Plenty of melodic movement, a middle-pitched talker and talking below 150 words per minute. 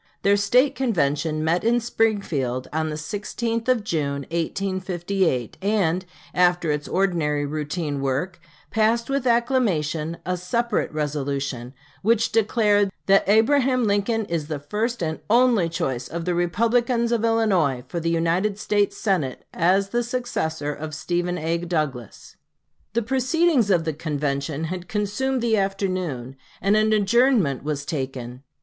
Yes: wide, 6.5 semitones; medium, 180 Hz; average, 140 wpm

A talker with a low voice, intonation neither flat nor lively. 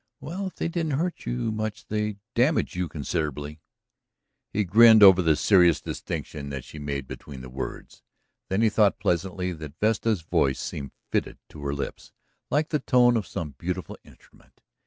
No: very low, 95 Hz; wide, 7.2 semitones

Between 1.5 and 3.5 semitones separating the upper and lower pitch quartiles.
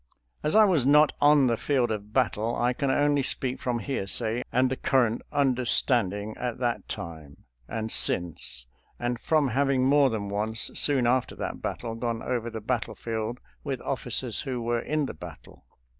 Yes: average, 3.2 semitones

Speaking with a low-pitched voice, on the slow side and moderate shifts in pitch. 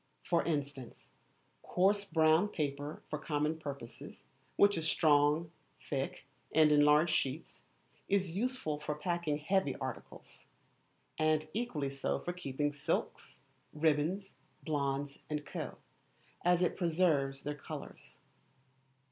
No: medium, 155 Hz; slow, 115 wpm; average, 3.0 semitones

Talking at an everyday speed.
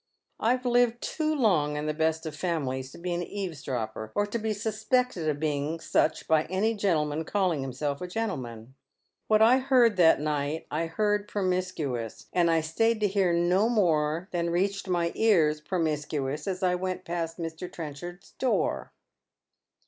Yes: average, 165 wpm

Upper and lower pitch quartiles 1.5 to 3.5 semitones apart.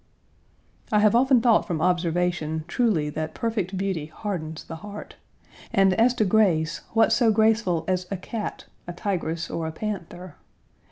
No: average, 4.7 semitones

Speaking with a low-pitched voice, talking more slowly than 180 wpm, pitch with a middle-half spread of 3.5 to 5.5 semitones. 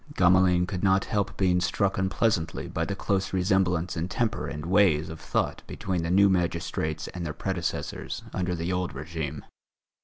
No: very low, 90 Hz; average, 165 wpm; narrow, 2.5 semitones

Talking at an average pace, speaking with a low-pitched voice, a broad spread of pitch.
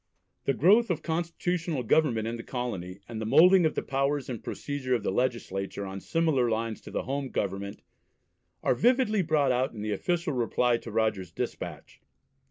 Yes: average, 175 wpm; low, 125 Hz; wide, 6.3 semitones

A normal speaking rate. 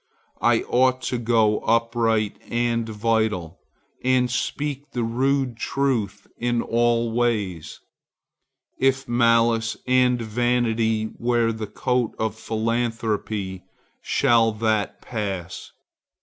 No: slow, 100 wpm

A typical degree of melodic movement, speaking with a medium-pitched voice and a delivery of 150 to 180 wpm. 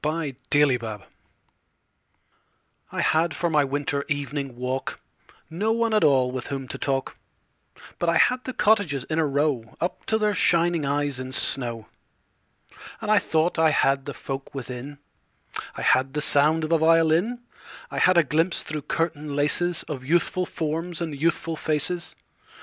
Yes: average, 3.7 semitones; medium, 150 Hz; average, 160 wpm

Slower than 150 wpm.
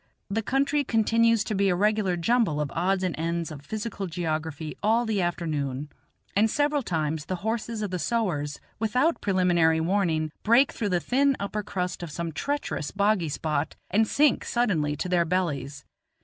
No: average, 170 wpm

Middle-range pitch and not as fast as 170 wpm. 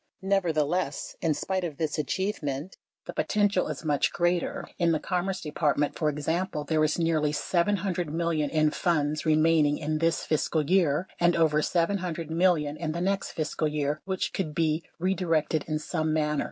Yes: medium, 160 Hz; average, 160 wpm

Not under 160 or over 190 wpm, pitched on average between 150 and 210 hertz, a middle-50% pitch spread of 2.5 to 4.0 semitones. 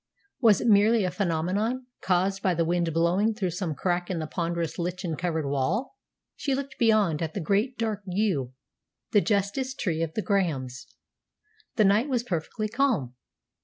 No: average, 165 wpm; high, 190 Hz; average, 4.5 semitones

